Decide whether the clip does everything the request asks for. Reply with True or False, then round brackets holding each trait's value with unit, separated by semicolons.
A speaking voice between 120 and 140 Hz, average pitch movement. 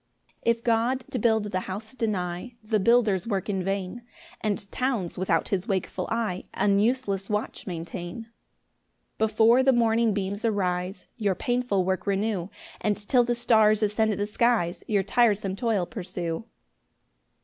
False (210 Hz; 3.3 semitones)